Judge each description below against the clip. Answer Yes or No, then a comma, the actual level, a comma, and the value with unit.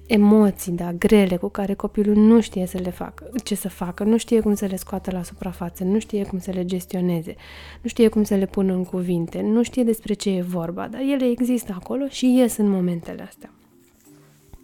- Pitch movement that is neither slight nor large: Yes, average, 3.2 semitones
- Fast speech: Yes, fast, 210 wpm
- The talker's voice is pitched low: No, high, 200 Hz